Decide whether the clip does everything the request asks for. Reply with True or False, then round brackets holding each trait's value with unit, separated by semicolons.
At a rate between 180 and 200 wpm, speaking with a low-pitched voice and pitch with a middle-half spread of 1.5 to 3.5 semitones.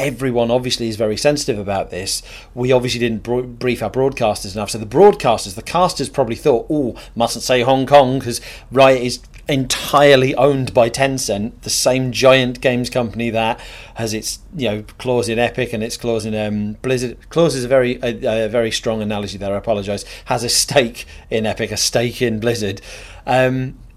True (190 wpm; 120 Hz; 2.7 semitones)